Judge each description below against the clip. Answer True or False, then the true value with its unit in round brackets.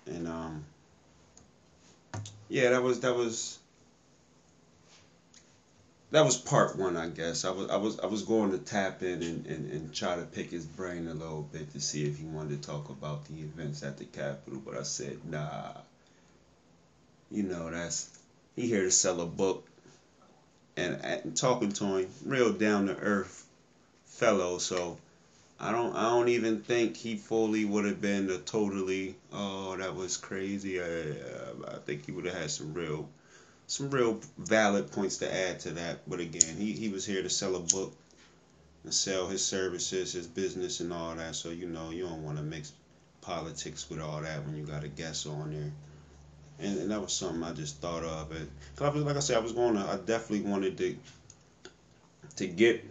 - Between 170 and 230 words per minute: True (190 wpm)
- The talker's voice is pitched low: True (85 Hz)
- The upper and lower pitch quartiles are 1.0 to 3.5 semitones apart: False (4.2 semitones)